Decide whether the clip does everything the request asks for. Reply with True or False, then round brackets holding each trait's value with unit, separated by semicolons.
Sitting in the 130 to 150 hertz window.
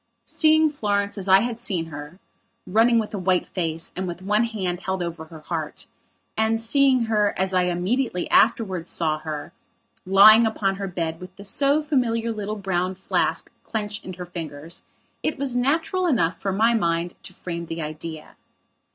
False (195 Hz)